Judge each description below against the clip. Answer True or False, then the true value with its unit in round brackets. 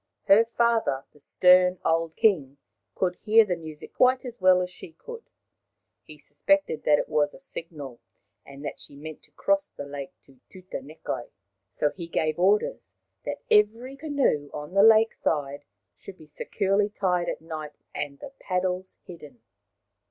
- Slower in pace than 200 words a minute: True (160 wpm)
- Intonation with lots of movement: True (5.9 semitones)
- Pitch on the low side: False (180 Hz)